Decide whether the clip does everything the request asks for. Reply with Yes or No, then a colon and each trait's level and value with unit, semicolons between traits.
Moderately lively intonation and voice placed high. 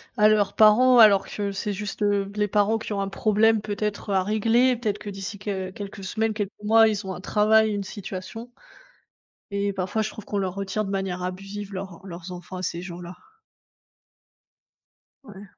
No: narrow, 1.9 semitones; high, 205 Hz